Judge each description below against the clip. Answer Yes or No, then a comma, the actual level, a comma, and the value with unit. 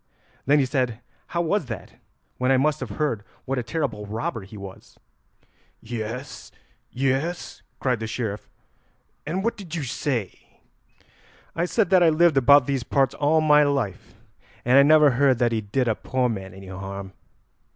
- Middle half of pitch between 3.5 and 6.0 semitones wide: Yes, average, 5.1 semitones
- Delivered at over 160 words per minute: Yes, average, 170 wpm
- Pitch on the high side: No, low, 130 Hz